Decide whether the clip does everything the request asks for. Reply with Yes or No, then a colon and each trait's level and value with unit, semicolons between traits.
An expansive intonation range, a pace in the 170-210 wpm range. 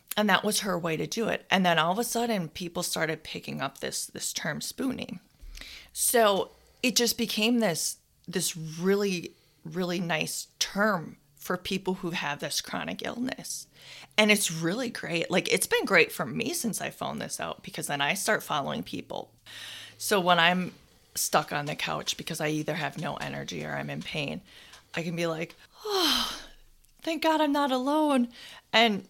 Yes: wide, 5.7 semitones; average, 180 wpm